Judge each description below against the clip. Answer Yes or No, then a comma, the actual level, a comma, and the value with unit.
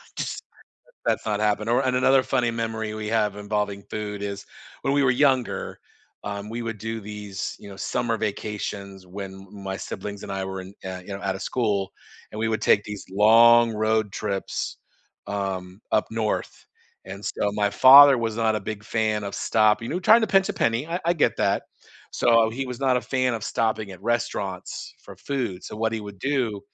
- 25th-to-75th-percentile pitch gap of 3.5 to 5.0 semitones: No, average, 2.7 semitones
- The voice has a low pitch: Yes, low, 110 Hz